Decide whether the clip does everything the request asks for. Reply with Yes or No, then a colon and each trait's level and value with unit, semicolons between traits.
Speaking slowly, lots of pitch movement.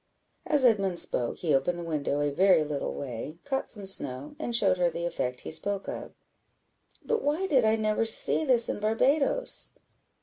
No: average, 180 wpm; wide, 7.9 semitones